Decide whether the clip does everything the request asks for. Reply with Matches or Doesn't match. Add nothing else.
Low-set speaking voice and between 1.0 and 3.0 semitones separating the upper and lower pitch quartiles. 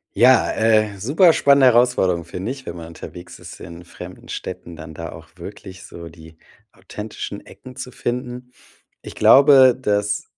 Doesn't match